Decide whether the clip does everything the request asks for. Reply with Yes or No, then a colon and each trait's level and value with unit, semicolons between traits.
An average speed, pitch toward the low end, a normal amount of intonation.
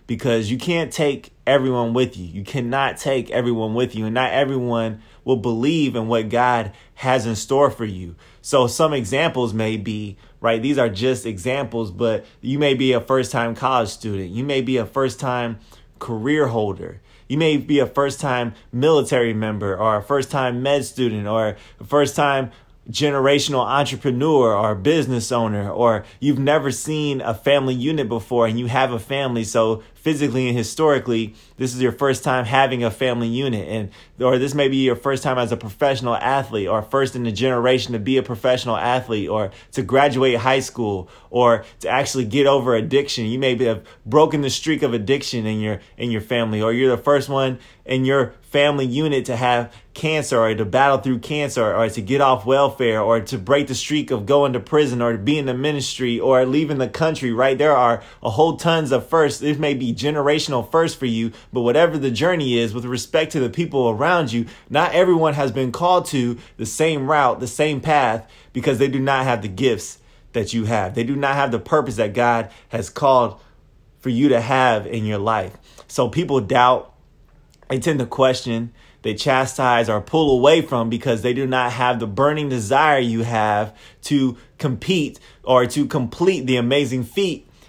Yes: average, 195 wpm; low, 125 Hz; average, 3.3 semitones